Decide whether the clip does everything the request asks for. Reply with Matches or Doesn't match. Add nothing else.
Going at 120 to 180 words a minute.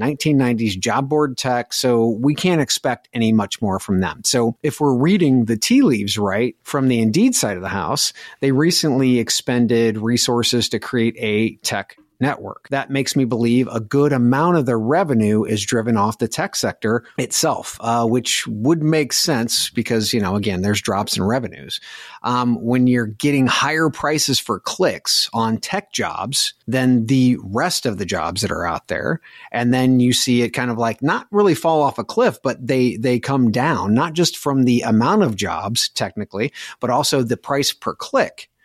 Doesn't match